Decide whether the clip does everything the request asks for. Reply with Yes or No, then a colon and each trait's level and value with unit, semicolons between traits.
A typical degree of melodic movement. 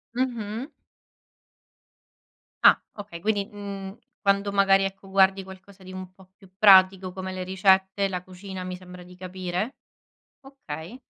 No: narrow, 1.4 semitones